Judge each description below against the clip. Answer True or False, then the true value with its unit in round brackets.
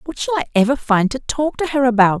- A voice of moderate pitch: False (255 Hz)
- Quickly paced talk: True (275 wpm)